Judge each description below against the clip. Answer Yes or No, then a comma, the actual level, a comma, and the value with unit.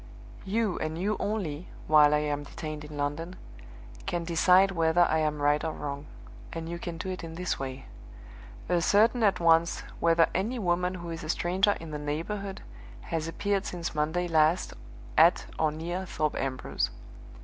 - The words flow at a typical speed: Yes, average, 170 wpm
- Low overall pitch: No, medium, 165 Hz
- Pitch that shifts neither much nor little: Yes, average, 3.0 semitones